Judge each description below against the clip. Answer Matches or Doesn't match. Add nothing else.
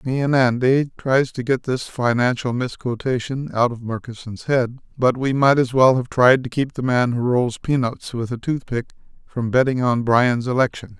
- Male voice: Matches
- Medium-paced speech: Matches